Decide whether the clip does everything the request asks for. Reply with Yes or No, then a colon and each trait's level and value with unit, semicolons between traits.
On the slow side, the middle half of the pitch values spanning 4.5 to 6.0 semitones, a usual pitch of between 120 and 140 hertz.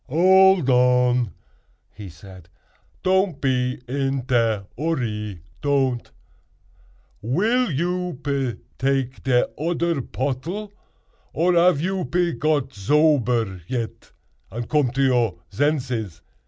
Yes: slow, 100 wpm; wide, 5.5 semitones; low, 135 Hz